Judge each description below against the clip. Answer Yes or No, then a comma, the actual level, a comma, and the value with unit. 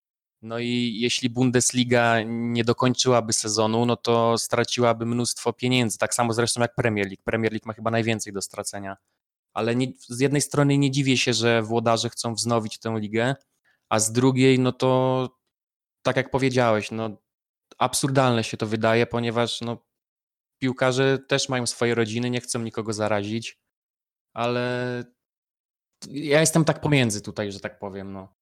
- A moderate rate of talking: Yes, average, 150 wpm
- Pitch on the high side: No, low, 120 Hz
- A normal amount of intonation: No, narrow, 2.0 semitones